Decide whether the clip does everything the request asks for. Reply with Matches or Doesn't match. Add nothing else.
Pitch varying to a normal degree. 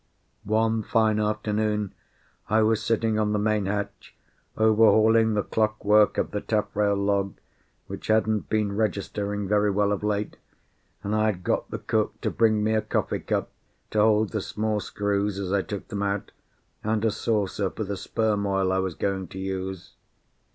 Doesn't match